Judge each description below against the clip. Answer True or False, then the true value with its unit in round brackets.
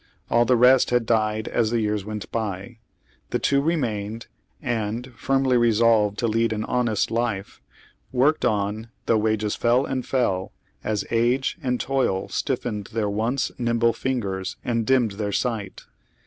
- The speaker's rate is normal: True (150 wpm)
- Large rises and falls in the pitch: False (2.6 semitones)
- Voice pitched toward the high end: False (115 Hz)